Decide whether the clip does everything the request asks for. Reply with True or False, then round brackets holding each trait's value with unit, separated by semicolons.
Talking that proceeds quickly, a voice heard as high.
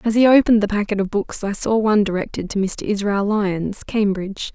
True (210 wpm; 205 Hz)